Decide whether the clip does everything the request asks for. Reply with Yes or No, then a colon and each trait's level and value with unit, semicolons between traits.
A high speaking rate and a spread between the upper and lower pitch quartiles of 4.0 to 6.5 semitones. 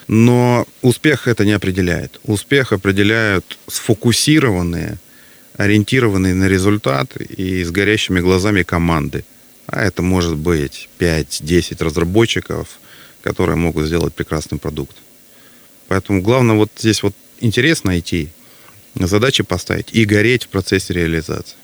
No: average, 115 wpm; average, 4.3 semitones